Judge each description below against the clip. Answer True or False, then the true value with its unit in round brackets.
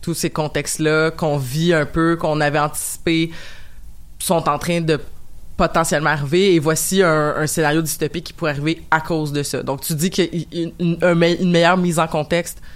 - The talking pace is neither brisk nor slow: True (200 wpm)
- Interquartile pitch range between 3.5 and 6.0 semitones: False (2.4 semitones)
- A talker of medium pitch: True (160 Hz)